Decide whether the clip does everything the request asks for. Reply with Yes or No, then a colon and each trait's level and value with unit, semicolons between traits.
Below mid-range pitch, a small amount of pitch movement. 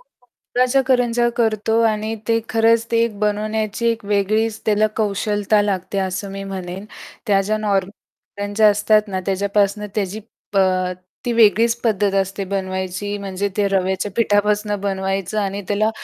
No: high, 205 Hz; narrow, 2.0 semitones